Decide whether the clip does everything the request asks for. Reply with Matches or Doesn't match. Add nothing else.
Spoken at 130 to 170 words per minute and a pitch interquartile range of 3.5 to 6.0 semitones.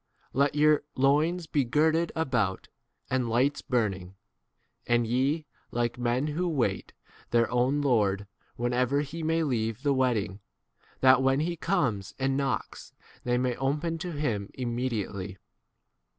Matches